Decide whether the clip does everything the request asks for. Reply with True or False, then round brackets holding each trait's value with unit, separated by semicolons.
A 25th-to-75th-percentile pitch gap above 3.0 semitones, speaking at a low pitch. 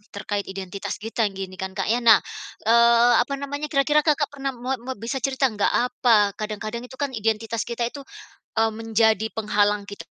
False (3.7 semitones; 225 Hz)